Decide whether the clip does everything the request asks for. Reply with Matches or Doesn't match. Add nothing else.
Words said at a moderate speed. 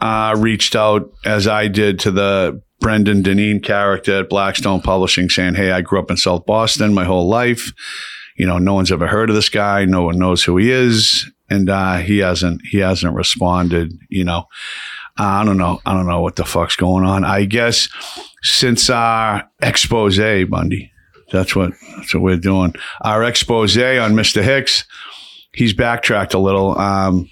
Matches